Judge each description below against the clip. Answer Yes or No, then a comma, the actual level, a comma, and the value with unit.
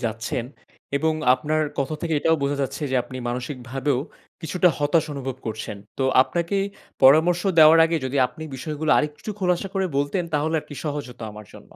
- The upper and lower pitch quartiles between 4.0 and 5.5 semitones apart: No, average, 3.5 semitones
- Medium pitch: Yes, medium, 150 Hz